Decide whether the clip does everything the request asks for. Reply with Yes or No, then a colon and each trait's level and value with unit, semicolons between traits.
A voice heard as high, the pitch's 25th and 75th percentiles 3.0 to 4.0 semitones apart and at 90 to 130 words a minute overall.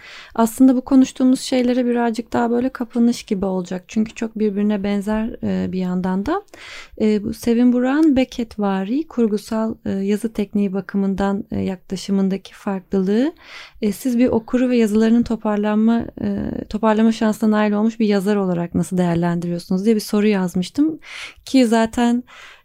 Yes: high, 220 Hz; average, 3.5 semitones; average, 125 wpm